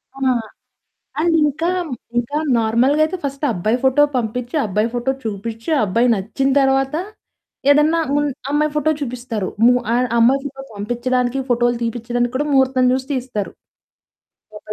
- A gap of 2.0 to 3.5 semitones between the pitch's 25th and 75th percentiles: Yes, average, 3.1 semitones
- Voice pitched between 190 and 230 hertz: No, very high, 250 Hz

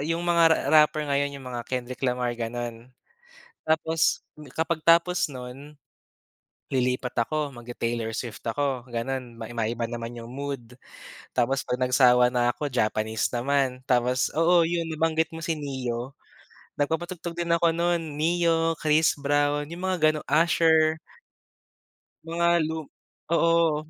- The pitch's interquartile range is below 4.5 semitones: No, average, 4.8 semitones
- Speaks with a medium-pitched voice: Yes, medium, 145 Hz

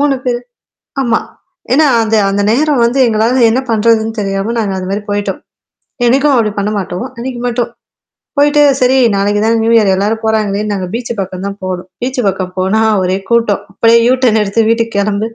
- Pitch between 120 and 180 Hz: No, high, 220 Hz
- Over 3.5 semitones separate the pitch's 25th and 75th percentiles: No, average, 3.2 semitones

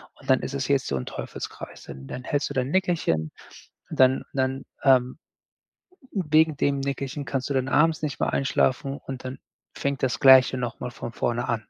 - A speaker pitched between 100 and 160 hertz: Yes, low, 135 Hz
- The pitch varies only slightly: Yes, narrow, 1.9 semitones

